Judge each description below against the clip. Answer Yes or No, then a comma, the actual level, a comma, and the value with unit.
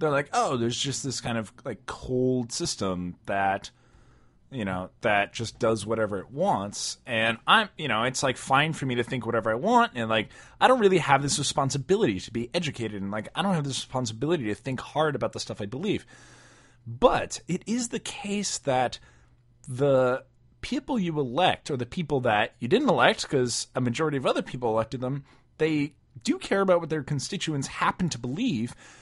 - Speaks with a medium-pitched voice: No, low, 130 Hz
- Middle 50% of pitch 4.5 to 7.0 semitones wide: Yes, average, 5.0 semitones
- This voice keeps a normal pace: Yes, average, 195 wpm